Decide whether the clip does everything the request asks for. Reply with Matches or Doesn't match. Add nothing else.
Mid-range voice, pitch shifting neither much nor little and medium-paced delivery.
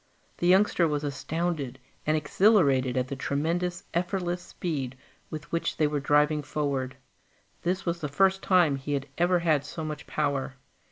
Matches